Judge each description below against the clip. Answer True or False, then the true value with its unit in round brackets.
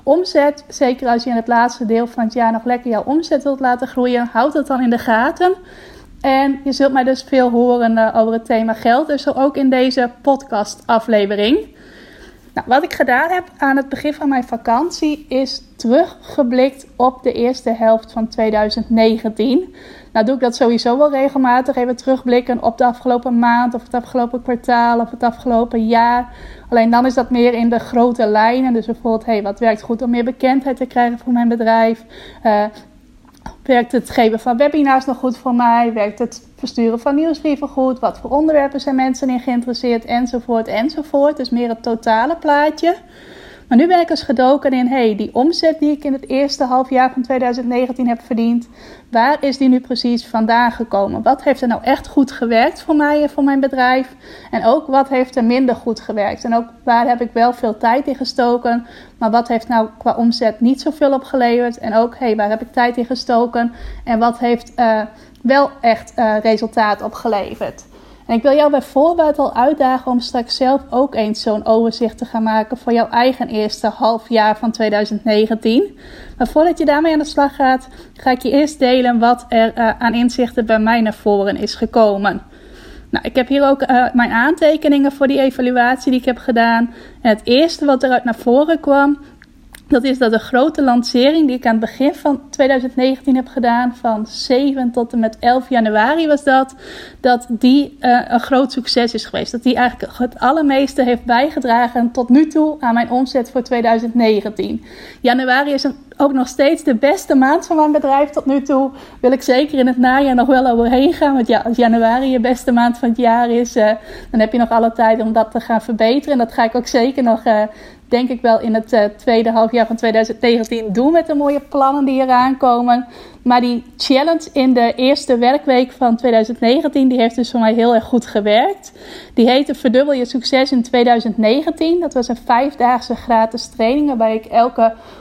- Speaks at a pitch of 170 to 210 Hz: False (245 Hz)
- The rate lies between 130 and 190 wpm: False (200 wpm)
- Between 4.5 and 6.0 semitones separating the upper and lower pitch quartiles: False (2.7 semitones)